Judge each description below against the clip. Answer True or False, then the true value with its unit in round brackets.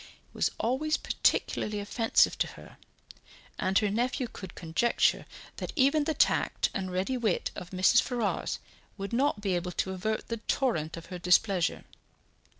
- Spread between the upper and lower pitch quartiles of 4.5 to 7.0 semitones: True (4.9 semitones)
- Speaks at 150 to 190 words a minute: True (155 wpm)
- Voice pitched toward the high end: True (210 Hz)